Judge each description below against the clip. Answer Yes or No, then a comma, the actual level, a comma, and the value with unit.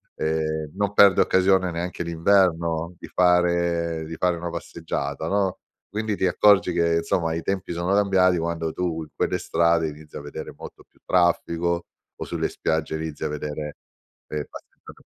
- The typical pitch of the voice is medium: No, very low, 85 Hz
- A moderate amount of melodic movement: No, narrow, 2.1 semitones